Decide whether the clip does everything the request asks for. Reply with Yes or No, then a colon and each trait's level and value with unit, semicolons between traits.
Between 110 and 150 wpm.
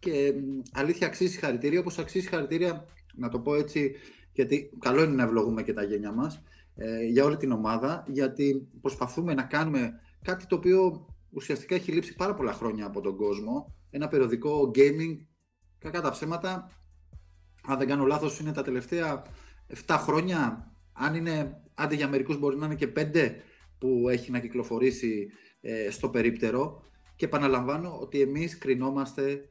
No: average, 165 wpm